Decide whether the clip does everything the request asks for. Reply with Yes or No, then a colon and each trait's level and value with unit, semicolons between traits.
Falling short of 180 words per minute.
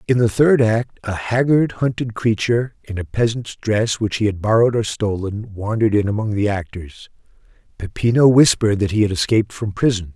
No: average, 185 wpm